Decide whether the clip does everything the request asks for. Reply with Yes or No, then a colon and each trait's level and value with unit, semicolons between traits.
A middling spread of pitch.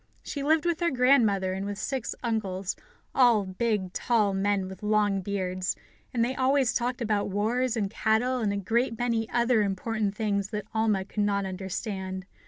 Yes: average, 3.4 semitones